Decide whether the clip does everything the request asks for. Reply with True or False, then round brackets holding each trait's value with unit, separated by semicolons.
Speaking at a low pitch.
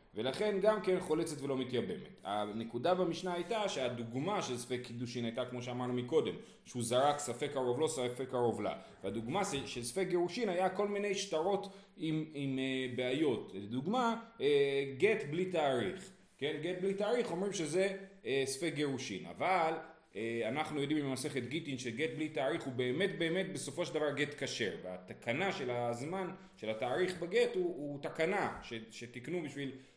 False (150 Hz)